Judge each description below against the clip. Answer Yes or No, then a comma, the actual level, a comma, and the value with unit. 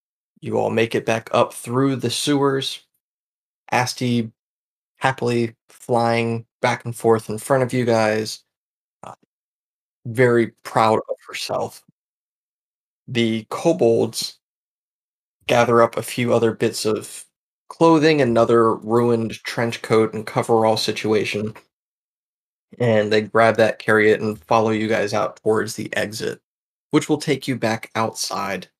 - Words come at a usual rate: No, slow, 130 wpm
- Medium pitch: No, low, 115 Hz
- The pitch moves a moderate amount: No, narrow, 2.2 semitones